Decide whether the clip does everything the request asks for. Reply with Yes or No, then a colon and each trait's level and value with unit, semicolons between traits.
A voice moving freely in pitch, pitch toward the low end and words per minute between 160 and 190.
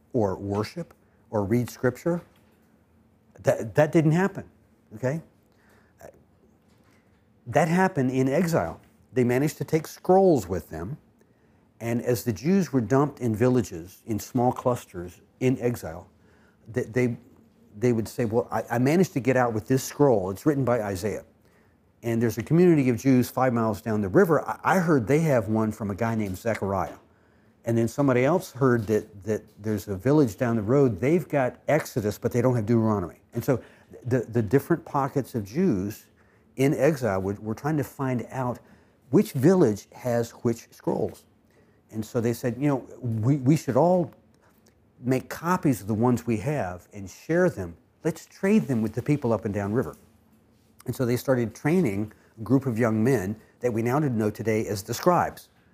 No: average, 4.0 semitones; low, 120 Hz; average, 180 wpm